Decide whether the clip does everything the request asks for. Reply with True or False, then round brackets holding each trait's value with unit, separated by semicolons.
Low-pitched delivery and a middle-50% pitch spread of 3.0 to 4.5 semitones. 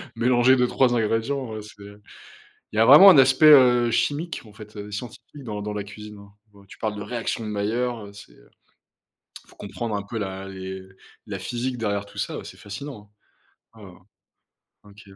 True (110 Hz; 3.3 semitones)